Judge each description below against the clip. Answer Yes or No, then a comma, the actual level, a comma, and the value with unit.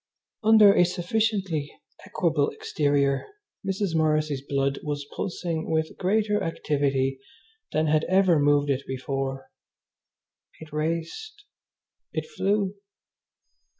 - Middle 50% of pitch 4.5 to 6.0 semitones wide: Yes, average, 5.2 semitones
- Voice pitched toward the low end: No, medium, 160 Hz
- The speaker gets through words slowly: Yes, slow, 100 wpm